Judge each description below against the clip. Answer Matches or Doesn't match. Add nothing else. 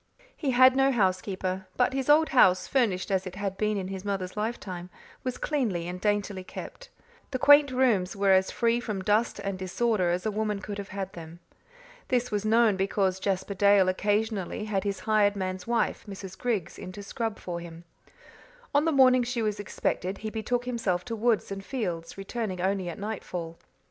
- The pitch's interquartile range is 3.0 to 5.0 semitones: Matches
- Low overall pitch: Doesn't match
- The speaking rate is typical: Matches